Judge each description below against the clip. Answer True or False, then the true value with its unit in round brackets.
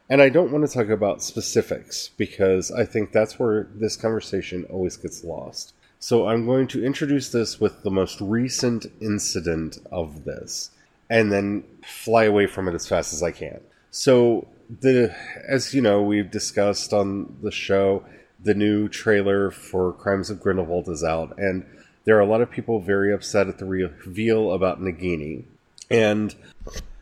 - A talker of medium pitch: False (100 Hz)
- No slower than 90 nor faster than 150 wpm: False (170 wpm)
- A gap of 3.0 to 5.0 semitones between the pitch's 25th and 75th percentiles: True (3.4 semitones)